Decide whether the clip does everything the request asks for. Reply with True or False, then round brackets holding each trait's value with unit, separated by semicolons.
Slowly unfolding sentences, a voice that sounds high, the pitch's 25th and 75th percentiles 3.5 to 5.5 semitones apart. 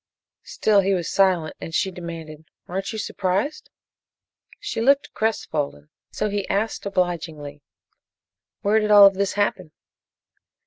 True (130 wpm; 195 Hz; 3.9 semitones)